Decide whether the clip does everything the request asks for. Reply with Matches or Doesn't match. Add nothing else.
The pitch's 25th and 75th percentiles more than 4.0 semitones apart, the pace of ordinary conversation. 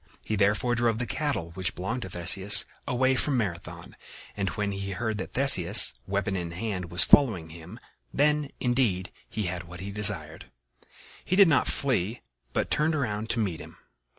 Matches